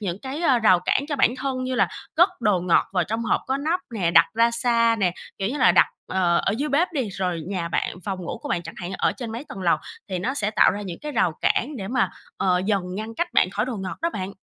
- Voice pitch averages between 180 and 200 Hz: No, high, 215 Hz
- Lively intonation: Yes, wide, 5.8 semitones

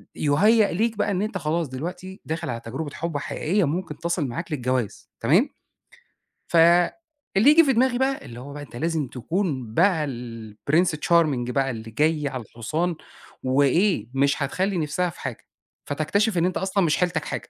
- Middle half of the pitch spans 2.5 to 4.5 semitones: No, average, 5.2 semitones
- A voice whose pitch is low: No, medium, 160 Hz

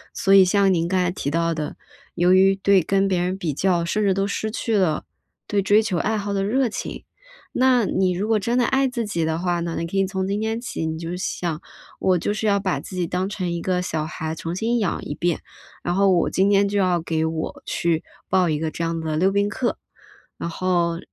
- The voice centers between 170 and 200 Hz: Yes, medium, 185 Hz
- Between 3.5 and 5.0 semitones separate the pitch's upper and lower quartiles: No, average, 3.1 semitones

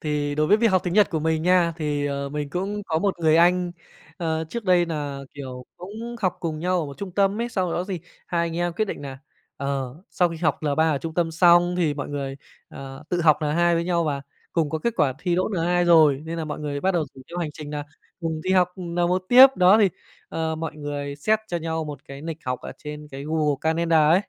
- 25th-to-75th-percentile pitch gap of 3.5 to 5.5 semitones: No, average, 3.1 semitones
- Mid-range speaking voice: Yes, medium, 165 Hz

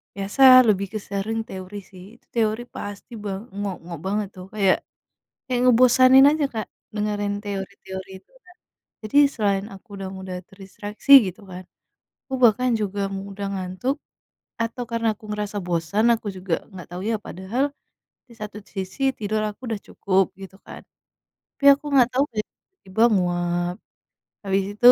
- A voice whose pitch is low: No, high, 205 Hz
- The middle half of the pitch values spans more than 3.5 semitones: No, average, 3.0 semitones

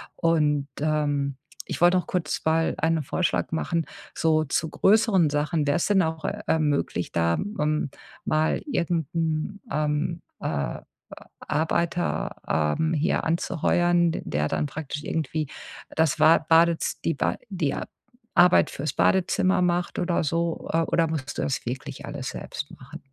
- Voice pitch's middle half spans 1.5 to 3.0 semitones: Yes, narrow, 2.5 semitones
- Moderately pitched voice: Yes, medium, 160 Hz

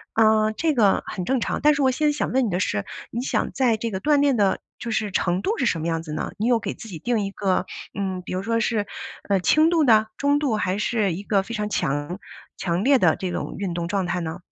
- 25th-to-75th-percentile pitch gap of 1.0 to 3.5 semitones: No, average, 4.9 semitones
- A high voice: Yes, high, 210 Hz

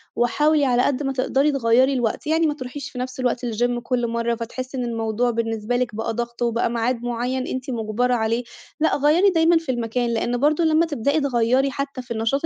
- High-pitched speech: Yes, very high, 250 Hz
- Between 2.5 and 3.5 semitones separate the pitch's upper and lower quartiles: Yes, average, 3.0 semitones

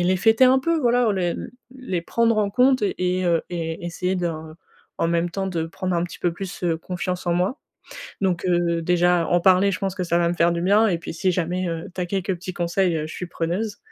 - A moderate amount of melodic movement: No, narrow, 2.3 semitones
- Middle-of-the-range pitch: Yes, medium, 180 Hz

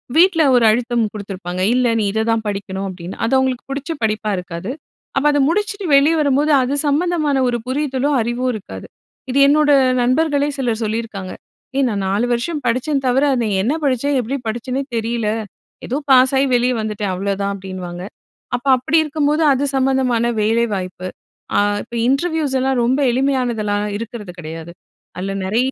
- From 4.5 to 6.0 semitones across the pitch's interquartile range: Yes, average, 4.8 semitones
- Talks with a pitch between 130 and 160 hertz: No, high, 245 Hz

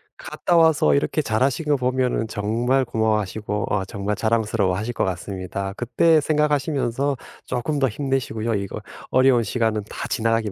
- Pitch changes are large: No, average, 4.4 semitones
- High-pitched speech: No, low, 115 Hz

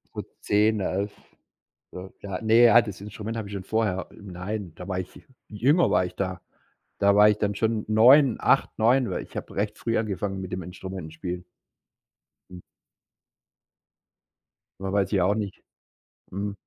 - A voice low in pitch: Yes, low, 100 Hz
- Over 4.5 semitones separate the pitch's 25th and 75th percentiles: No, average, 2.7 semitones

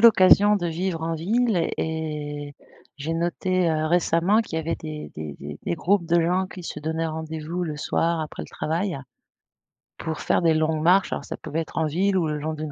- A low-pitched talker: No, medium, 165 Hz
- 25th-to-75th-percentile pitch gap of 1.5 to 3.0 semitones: Yes, narrow, 2.5 semitones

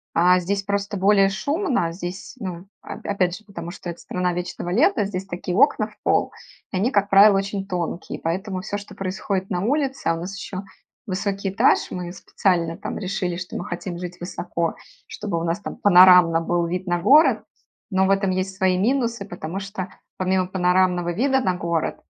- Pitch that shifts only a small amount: Yes, narrow, 2.1 semitones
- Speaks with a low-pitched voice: No, medium, 185 Hz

